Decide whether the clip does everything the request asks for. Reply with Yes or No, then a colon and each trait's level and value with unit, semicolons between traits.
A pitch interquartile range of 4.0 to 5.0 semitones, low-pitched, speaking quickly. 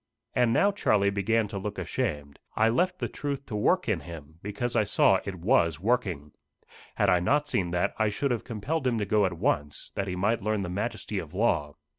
Yes: average, 4.7 semitones; low, 105 Hz; fast, 215 wpm